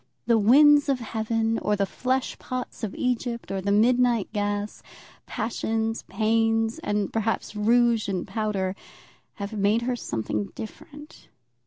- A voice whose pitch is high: Yes, high, 225 Hz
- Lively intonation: No, narrow, 2.6 semitones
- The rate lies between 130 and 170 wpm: Yes, slow, 135 wpm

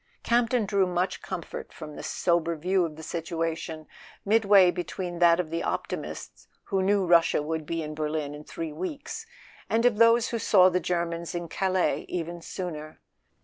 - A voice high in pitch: No, medium, 175 Hz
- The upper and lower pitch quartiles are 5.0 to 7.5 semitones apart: No, average, 2.9 semitones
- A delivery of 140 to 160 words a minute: No, average, 175 wpm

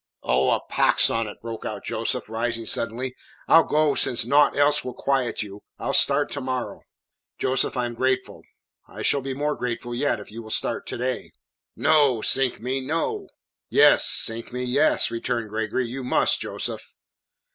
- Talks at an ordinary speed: Yes, average, 175 wpm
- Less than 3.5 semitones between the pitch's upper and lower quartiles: Yes, average, 3.1 semitones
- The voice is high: No, low, 125 Hz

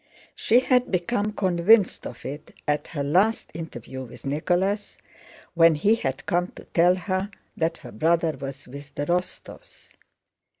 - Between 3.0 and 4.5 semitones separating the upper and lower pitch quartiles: No, average, 4.9 semitones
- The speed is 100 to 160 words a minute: Yes, average, 145 wpm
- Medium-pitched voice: Yes, medium, 170 Hz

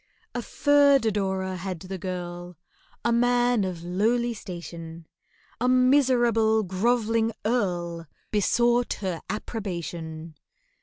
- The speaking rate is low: Yes, slow, 100 wpm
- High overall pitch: Yes, high, 205 Hz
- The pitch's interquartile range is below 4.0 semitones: No, average, 5.2 semitones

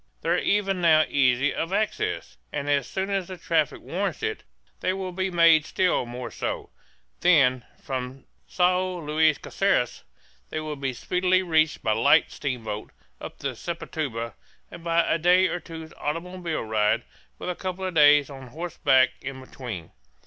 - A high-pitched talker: No, medium, 160 Hz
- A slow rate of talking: No, average, 165 wpm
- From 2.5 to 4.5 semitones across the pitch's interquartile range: No, average, 5.3 semitones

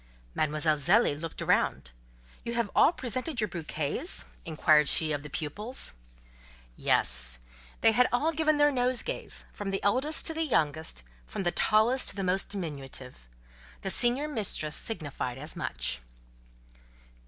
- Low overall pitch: No, high, 195 Hz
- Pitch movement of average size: No, wide, 8.7 semitones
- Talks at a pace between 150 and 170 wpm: No, average, 140 wpm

